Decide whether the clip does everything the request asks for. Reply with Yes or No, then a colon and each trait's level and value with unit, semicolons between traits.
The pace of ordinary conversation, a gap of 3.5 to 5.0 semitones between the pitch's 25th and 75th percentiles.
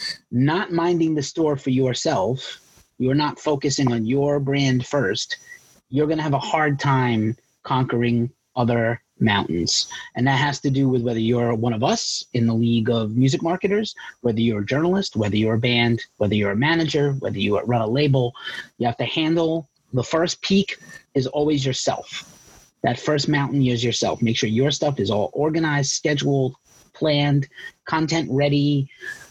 Yes: average, 170 wpm; average, 4.0 semitones